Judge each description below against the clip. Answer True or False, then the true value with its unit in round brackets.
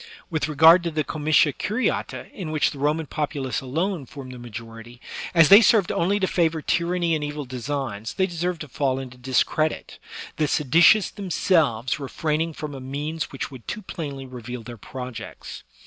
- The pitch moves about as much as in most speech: True (4.3 semitones)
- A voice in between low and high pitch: True (150 Hz)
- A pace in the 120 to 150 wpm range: False (180 wpm)